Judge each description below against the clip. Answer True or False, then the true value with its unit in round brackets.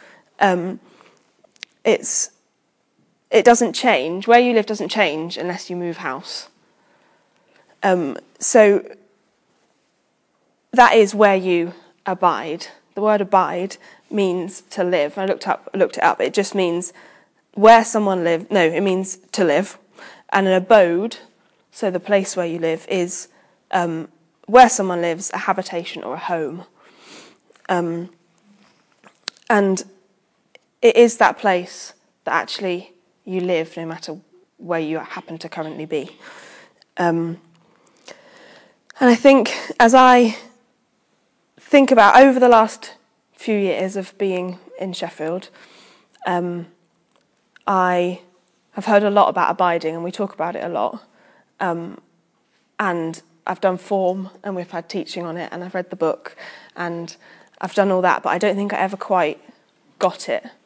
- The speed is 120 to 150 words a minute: True (140 wpm)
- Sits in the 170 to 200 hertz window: True (185 Hz)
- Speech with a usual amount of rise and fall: True (3.0 semitones)